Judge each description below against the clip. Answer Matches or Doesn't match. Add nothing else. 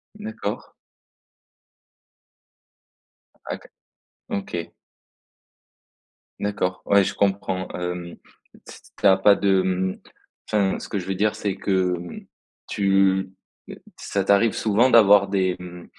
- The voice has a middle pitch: Doesn't match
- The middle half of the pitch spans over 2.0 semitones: Doesn't match